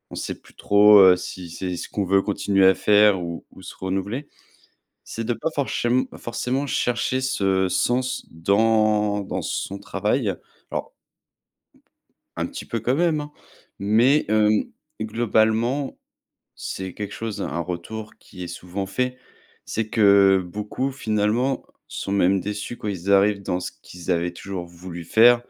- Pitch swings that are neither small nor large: Yes, average, 3.7 semitones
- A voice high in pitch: No, low, 105 Hz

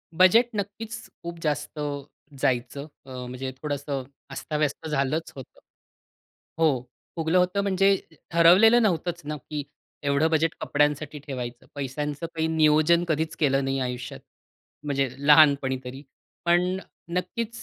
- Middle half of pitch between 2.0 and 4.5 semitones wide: Yes, average, 3.7 semitones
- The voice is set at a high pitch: No, medium, 150 Hz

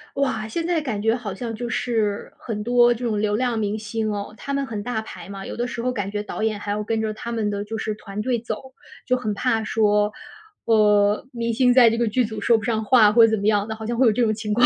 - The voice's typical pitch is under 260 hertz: Yes, high, 220 Hz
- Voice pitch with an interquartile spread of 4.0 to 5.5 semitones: No, narrow, 2.4 semitones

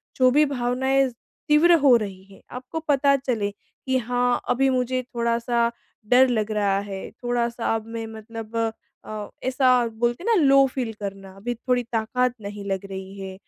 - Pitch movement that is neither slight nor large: Yes, average, 3.5 semitones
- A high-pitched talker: Yes, high, 240 Hz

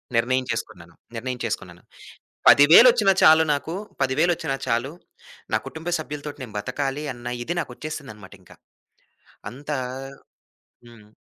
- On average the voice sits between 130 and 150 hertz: Yes, low, 135 Hz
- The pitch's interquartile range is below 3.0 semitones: No, average, 4.5 semitones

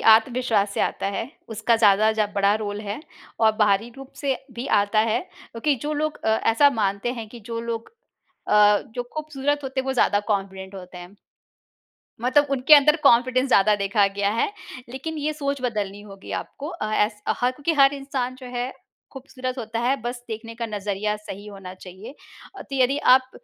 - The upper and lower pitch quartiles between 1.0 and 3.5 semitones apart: No, average, 4.2 semitones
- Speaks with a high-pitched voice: Yes, high, 230 Hz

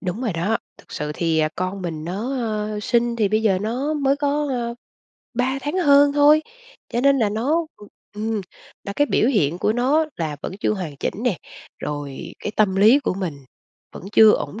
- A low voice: No, high, 220 Hz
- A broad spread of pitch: Yes, wide, 6.5 semitones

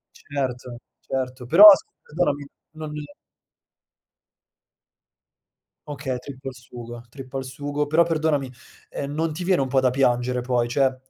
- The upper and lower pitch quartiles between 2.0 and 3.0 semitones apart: Yes, average, 2.7 semitones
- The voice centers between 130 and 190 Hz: Yes, low, 135 Hz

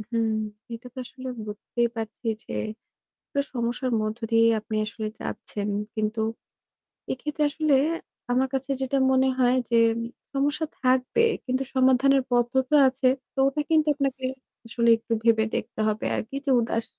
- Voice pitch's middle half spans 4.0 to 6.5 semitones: No, average, 2.9 semitones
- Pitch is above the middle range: Yes, very high, 255 Hz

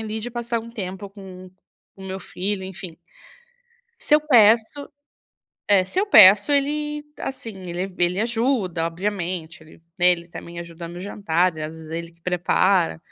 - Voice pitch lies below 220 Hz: Yes, high, 190 Hz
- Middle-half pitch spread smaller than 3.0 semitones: No, average, 4.6 semitones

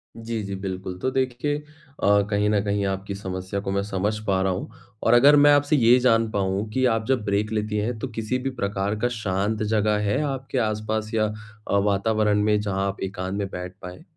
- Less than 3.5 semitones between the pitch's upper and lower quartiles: Yes, average, 2.8 semitones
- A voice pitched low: Yes, low, 105 Hz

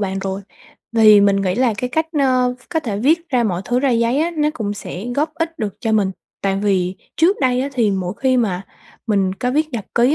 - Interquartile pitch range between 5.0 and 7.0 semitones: Yes, wide, 5.6 semitones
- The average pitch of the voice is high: Yes, high, 235 Hz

